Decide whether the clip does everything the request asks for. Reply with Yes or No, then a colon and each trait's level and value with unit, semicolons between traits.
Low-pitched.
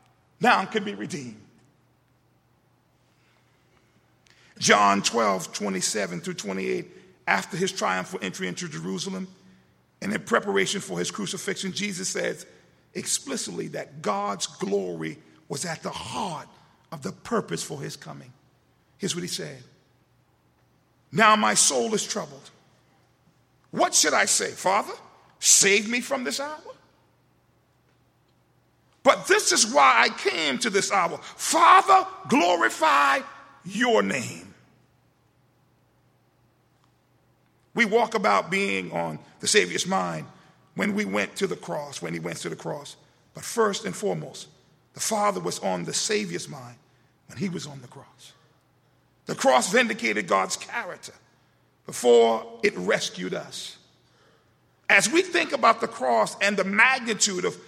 No: high, 190 Hz